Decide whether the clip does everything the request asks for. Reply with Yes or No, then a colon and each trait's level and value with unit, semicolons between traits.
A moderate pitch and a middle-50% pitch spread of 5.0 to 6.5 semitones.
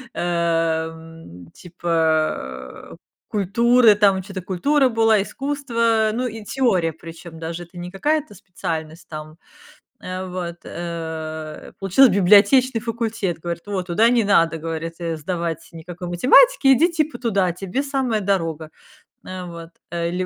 Yes: medium, 180 Hz; wide, 5.4 semitones